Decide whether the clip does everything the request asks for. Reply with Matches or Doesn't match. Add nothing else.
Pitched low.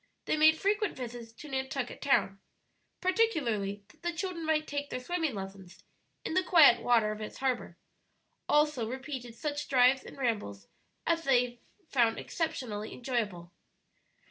Doesn't match